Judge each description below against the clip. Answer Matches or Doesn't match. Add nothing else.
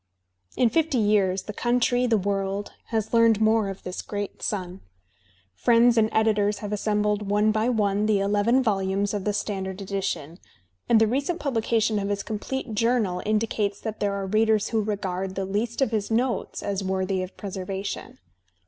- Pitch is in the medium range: Doesn't match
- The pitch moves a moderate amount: Doesn't match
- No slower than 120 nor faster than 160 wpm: Doesn't match